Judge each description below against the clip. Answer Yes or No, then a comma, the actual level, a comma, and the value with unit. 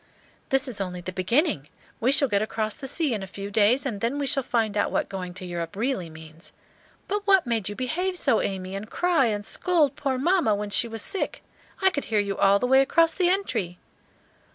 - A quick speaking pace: Yes, fast, 225 wpm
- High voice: Yes, high, 225 Hz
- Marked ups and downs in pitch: Yes, wide, 6.2 semitones